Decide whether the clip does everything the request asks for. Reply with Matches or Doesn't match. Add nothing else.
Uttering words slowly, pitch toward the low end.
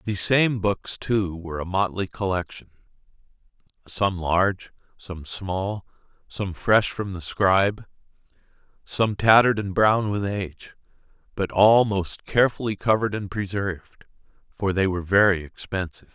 Matches